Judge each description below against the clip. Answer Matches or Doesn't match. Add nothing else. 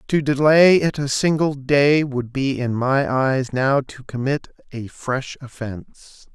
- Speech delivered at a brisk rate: Doesn't match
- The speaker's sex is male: Matches